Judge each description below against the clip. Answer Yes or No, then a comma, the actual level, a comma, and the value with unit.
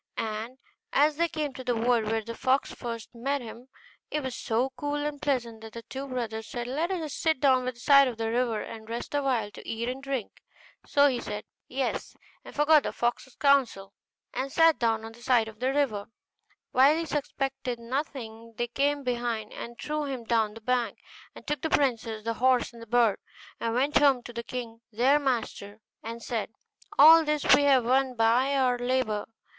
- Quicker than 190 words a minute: Yes, fast, 205 wpm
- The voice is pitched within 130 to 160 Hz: No, very high, 250 Hz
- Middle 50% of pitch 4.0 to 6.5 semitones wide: No, average, 3.3 semitones